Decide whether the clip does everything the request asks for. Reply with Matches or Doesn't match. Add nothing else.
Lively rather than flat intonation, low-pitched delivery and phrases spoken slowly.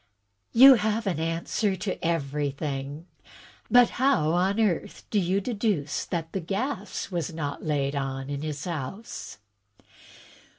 Doesn't match